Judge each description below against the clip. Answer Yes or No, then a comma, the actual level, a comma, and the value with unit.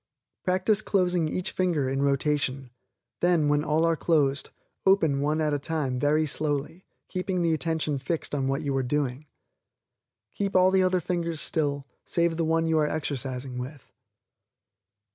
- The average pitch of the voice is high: No, medium, 155 Hz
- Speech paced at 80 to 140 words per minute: No, average, 160 wpm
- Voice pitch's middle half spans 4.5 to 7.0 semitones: No, average, 3.4 semitones